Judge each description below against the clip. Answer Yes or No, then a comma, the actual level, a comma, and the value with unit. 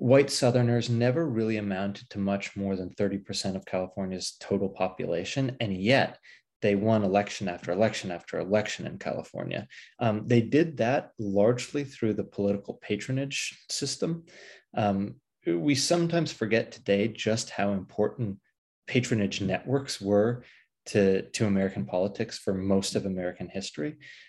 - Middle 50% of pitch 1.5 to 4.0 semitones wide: Yes, average, 3.7 semitones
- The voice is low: Yes, low, 105 Hz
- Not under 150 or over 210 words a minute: No, slow, 135 wpm